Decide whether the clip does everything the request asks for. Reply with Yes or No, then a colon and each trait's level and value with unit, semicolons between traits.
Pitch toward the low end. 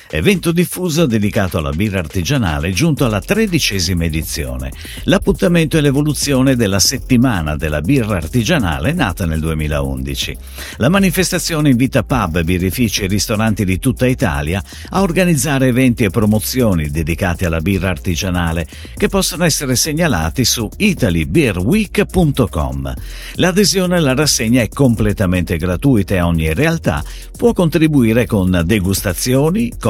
Yes: low, 110 Hz